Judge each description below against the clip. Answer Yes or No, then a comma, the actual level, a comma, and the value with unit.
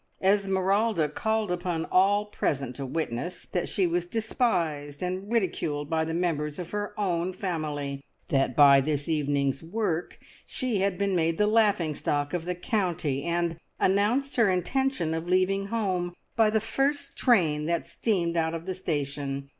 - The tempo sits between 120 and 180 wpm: Yes, average, 160 wpm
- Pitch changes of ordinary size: Yes, average, 4.8 semitones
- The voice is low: No, medium, 175 Hz